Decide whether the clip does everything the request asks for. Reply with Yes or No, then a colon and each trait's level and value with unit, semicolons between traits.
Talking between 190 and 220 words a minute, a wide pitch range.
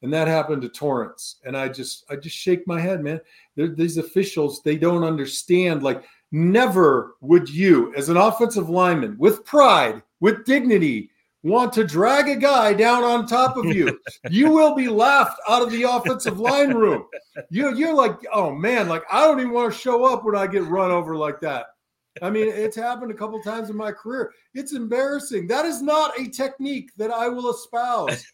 Yes: average, 195 wpm; wide, 6.6 semitones